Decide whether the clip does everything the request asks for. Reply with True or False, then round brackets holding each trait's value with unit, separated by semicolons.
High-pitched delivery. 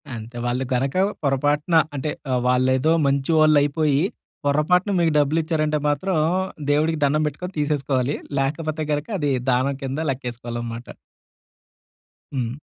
False (145 Hz)